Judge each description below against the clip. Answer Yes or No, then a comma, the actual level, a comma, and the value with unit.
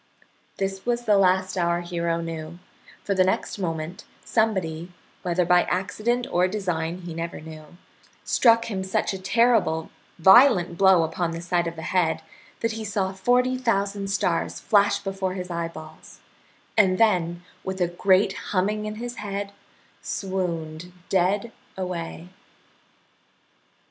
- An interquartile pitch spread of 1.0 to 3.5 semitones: Yes, average, 2.9 semitones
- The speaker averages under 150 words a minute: Yes, average, 140 wpm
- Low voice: No, medium, 185 Hz